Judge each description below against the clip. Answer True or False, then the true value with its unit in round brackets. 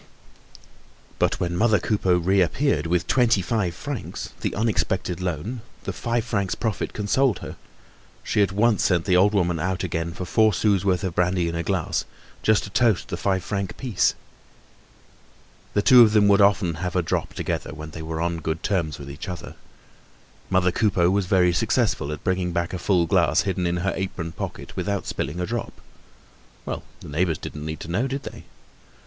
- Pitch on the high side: False (95 Hz)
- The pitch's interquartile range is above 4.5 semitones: False (3.2 semitones)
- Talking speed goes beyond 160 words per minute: True (190 wpm)